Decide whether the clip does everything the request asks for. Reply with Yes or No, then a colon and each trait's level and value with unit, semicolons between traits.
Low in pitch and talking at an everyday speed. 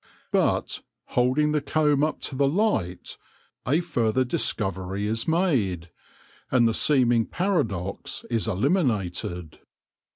No: low, 125 Hz; slow, 110 wpm